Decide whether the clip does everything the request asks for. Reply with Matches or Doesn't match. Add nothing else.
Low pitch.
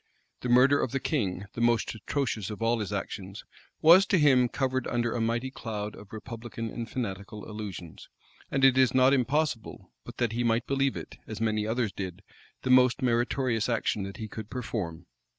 Matches